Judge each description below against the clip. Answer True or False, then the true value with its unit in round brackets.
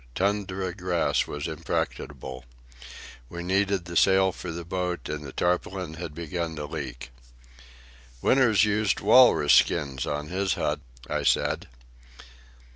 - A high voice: False (85 Hz)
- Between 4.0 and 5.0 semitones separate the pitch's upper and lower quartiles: True (4.4 semitones)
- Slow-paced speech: True (125 wpm)